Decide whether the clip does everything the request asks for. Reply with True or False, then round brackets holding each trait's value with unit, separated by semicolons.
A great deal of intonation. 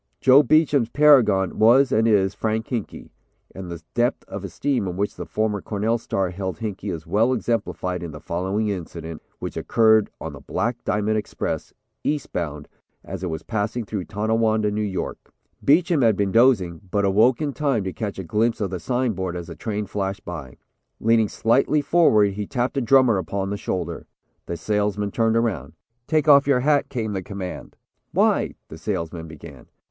False (4.0 semitones)